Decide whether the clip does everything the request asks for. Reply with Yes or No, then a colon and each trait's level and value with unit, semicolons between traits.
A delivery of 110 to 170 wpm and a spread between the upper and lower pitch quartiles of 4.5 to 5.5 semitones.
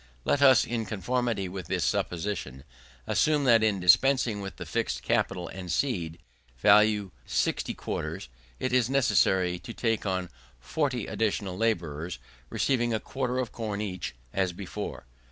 Yes: average, 145 wpm; average, 5.1 semitones